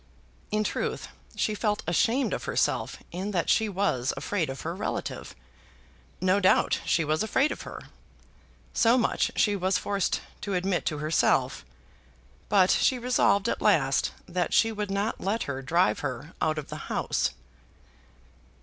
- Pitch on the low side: No, high, 195 Hz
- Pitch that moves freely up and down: No, average, 4.4 semitones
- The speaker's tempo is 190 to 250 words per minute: No, average, 155 wpm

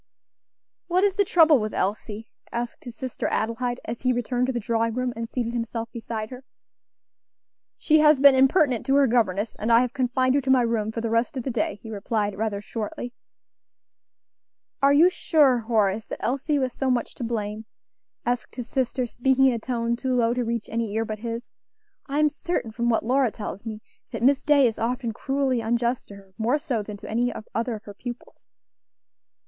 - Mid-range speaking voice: No, high, 240 Hz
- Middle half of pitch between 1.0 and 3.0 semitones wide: Yes, average, 2.7 semitones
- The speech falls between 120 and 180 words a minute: No, average, 200 wpm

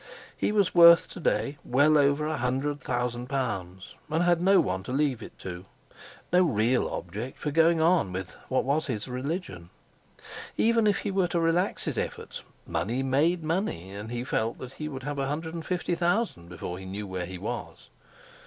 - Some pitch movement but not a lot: No, wide, 7.2 semitones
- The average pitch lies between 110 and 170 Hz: Yes, medium, 140 Hz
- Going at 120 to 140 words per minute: No, average, 190 wpm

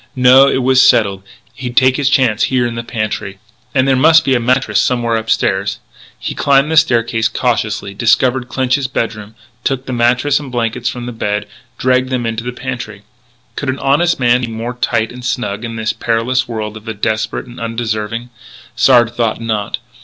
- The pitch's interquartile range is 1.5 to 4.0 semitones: Yes, narrow, 2.5 semitones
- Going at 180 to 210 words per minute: Yes, average, 185 wpm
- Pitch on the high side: No, low, 120 Hz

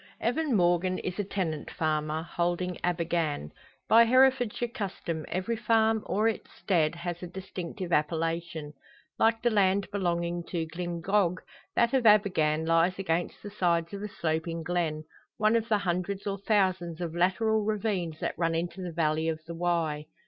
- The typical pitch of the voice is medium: Yes, medium, 175 Hz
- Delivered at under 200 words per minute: Yes, average, 160 wpm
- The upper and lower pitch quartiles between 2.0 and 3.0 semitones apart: No, average, 3.7 semitones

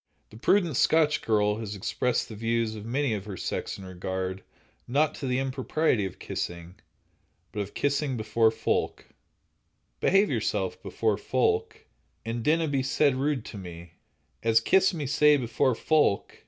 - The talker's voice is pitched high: No, low, 115 Hz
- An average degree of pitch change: No, wide, 5.9 semitones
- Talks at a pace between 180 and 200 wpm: No, average, 155 wpm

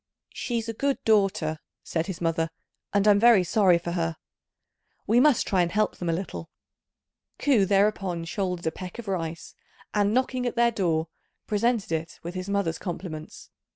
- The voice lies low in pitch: No, high, 190 Hz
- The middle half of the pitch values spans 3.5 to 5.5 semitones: Yes, average, 4.3 semitones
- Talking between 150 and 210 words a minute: Yes, average, 170 wpm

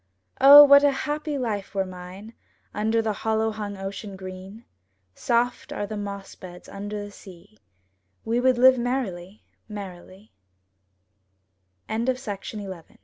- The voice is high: Yes, high, 210 Hz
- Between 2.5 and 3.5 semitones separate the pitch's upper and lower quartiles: No, average, 3.9 semitones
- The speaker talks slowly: Yes, slow, 120 wpm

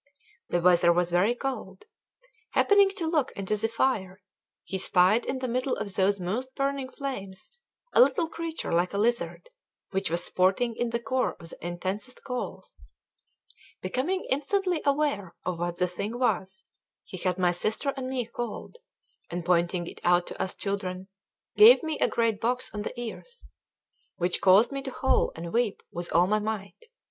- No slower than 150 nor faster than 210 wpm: Yes, average, 175 wpm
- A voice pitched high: Yes, high, 215 Hz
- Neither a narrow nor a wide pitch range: No, wide, 6.1 semitones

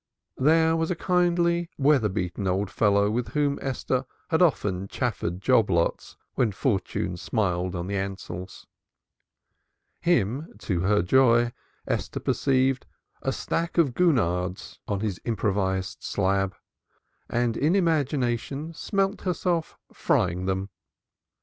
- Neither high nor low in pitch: No, low, 115 Hz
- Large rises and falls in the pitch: Yes, wide, 8.1 semitones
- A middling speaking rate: No, slow, 125 wpm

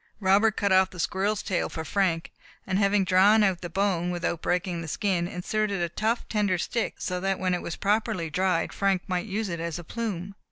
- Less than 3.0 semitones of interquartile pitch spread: Yes, narrow, 2.6 semitones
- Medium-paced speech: No, fast, 210 wpm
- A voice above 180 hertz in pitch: Yes, high, 190 Hz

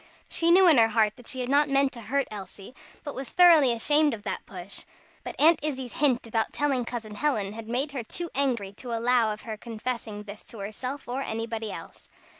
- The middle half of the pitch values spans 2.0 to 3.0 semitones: No, average, 4.3 semitones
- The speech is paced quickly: Yes, fast, 215 wpm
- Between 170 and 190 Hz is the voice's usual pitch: No, high, 240 Hz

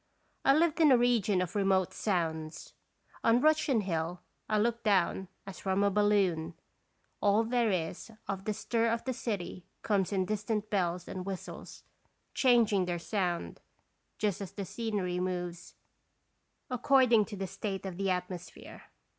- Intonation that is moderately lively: Yes, average, 3.7 semitones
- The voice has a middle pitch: No, high, 200 Hz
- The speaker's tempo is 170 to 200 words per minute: No, average, 155 wpm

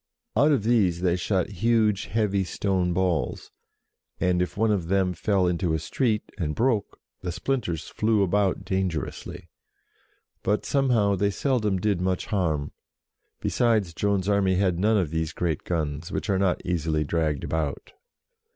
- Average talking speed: Yes, average, 155 wpm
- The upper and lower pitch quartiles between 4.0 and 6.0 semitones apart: No, average, 3.5 semitones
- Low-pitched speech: Yes, very low, 95 Hz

